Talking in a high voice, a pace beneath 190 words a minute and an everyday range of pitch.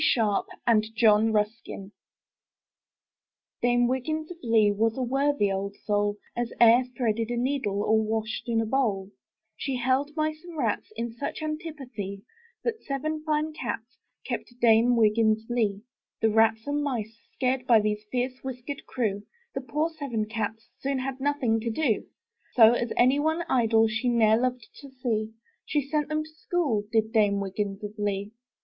Yes: high, 235 Hz; average, 170 wpm; average, 3.8 semitones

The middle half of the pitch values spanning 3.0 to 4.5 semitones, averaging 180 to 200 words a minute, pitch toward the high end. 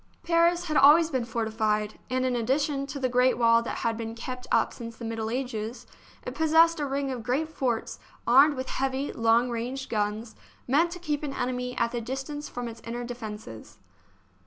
Yes: average, 3.4 semitones; average, 195 wpm; very high, 250 Hz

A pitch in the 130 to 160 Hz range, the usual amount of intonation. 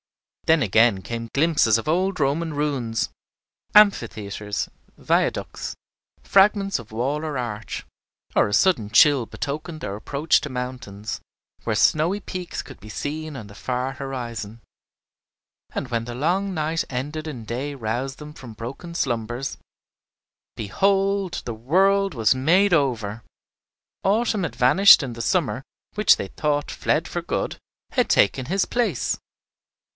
No: low, 135 Hz; wide, 6.2 semitones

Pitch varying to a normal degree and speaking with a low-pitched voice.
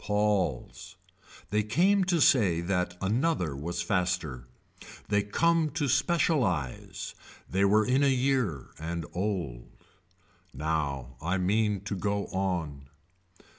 No: wide, 6.8 semitones; low, 100 Hz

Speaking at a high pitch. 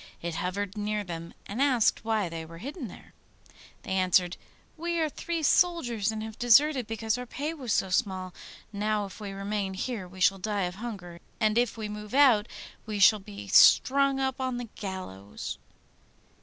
Yes: high, 210 Hz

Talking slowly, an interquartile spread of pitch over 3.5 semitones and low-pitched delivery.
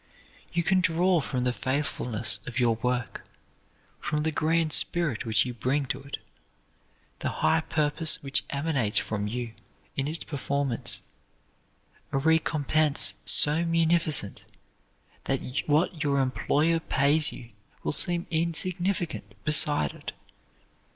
No: slow, 125 wpm; average, 4.1 semitones; medium, 145 Hz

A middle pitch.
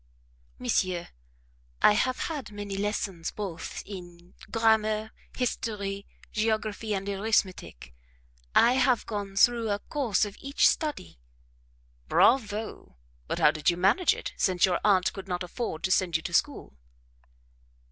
No: high, 205 Hz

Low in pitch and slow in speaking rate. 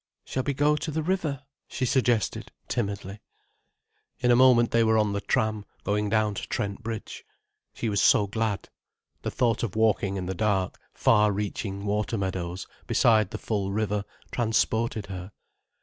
No: low, 110 Hz; average, 165 wpm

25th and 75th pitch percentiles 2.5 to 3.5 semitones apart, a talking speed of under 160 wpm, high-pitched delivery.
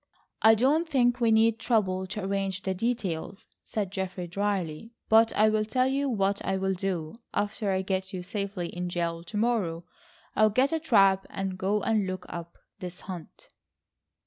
No: average, 3.1 semitones; average, 170 wpm; high, 195 Hz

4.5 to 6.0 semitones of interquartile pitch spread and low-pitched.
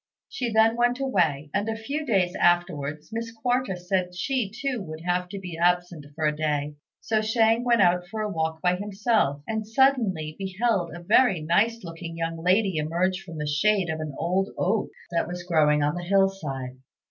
No: average, 5.2 semitones; medium, 180 Hz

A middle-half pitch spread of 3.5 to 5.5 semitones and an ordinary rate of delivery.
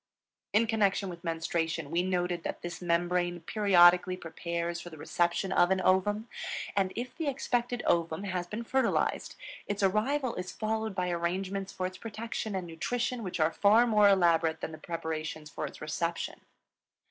Yes: average, 3.8 semitones; average, 165 wpm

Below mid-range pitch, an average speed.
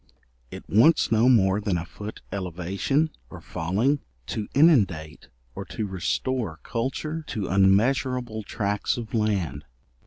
No: low, 105 Hz; slow, 125 wpm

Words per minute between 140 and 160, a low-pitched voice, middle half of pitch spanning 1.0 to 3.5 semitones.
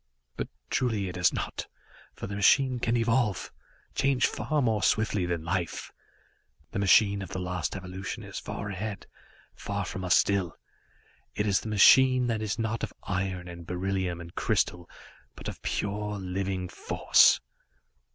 Yes: average, 155 wpm; low, 100 Hz; average, 3.1 semitones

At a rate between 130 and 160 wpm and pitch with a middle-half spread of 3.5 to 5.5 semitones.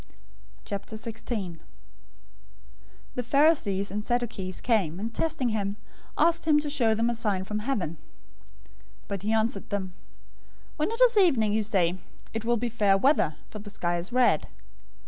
Yes: average, 155 wpm; average, 3.9 semitones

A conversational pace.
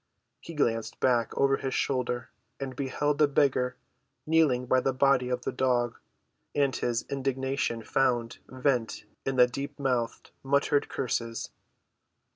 No: slow, 130 wpm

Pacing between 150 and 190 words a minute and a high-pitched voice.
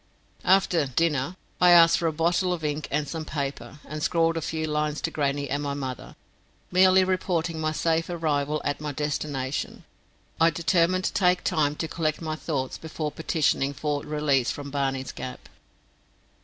No: average, 170 wpm; medium, 155 Hz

